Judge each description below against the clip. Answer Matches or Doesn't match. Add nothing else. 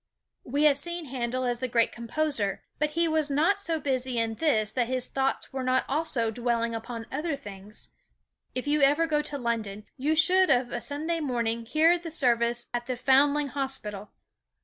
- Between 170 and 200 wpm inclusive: Matches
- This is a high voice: Matches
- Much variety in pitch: Doesn't match